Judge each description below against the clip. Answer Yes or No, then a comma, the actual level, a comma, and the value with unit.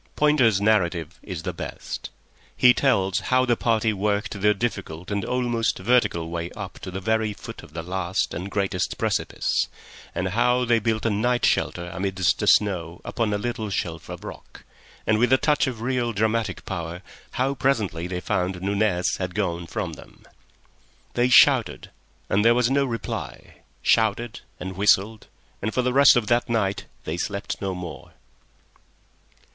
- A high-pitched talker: No, low, 105 Hz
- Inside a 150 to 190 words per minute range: Yes, average, 170 wpm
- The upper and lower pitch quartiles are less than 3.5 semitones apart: No, average, 4.3 semitones